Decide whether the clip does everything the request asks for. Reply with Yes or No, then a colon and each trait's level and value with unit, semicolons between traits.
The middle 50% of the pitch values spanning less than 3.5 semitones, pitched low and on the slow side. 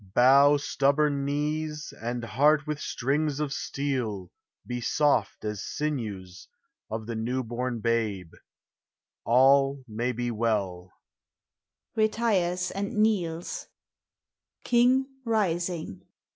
No: average, 4.3 semitones; low, 125 Hz; slow, 85 wpm